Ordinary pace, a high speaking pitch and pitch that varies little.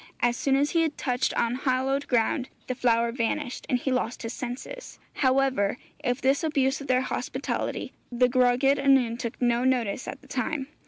Yes: average, 175 wpm; very high, 255 Hz; narrow, 2.0 semitones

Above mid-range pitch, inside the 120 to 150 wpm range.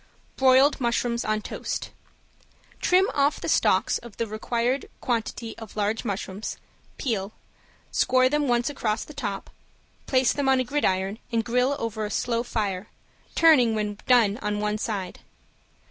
Yes: high, 235 Hz; average, 145 wpm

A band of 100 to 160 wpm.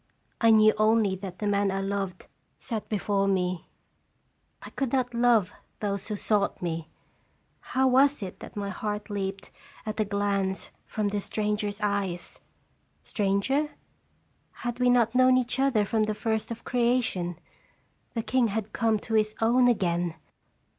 Yes: average, 155 wpm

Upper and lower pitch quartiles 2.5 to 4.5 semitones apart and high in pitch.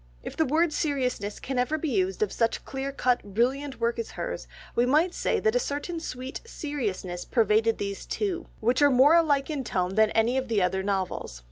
No: wide, 5.4 semitones; very high, 250 Hz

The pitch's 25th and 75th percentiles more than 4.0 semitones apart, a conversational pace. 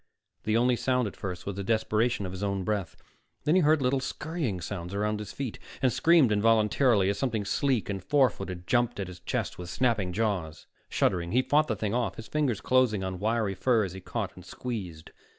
No: average, 4.7 semitones; fast, 210 wpm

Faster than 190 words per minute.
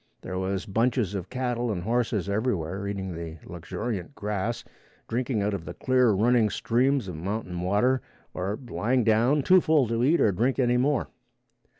No: average, 170 wpm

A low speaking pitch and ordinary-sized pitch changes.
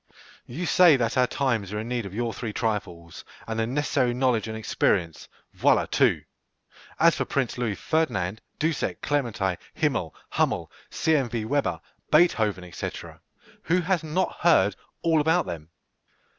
No: low, 120 Hz; wide, 6.2 semitones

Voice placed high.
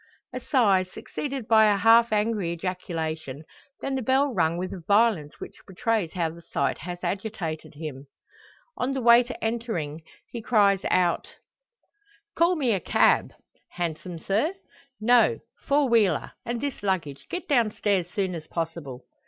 Yes: high, 200 Hz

